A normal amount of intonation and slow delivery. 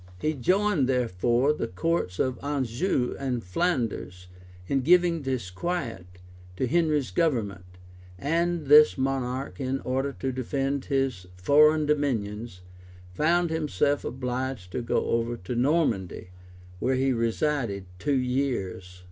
Yes: average, 4.5 semitones; slow, 120 wpm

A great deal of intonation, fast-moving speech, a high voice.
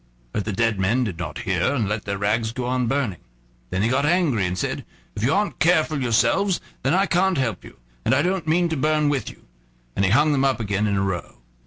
No: wide, 6.8 semitones; fast, 240 wpm; low, 125 Hz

